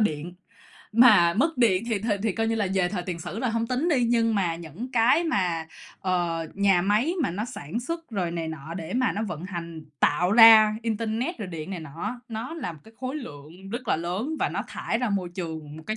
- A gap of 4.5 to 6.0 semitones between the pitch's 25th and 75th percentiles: Yes, wide, 5.4 semitones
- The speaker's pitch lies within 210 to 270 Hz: No, high, 200 Hz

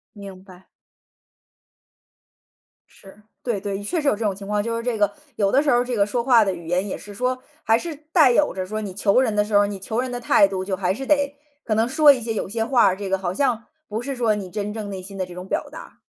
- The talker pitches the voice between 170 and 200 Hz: No, high, 210 Hz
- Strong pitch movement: No, average, 3.9 semitones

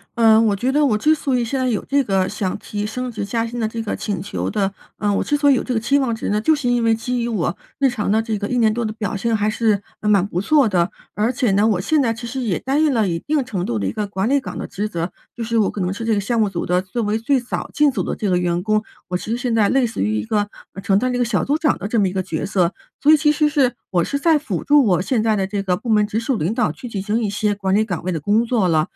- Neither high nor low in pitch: No, high, 220 Hz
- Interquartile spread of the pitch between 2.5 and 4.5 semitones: Yes, average, 4.0 semitones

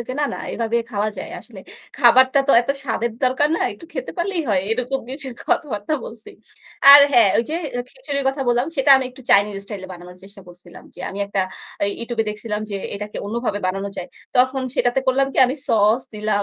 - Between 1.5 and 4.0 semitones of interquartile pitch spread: No, average, 4.4 semitones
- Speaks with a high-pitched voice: Yes, high, 235 Hz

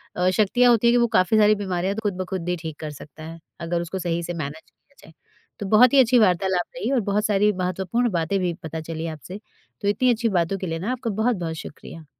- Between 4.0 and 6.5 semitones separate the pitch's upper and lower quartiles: Yes, average, 4.7 semitones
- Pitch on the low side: No, high, 190 Hz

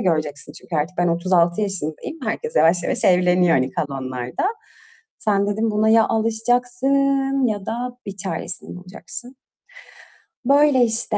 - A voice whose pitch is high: Yes, high, 205 Hz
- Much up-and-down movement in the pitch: Yes, wide, 6.0 semitones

